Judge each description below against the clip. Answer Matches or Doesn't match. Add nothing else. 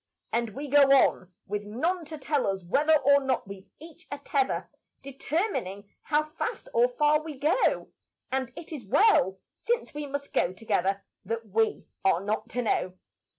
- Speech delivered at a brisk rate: Doesn't match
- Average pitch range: Doesn't match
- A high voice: Matches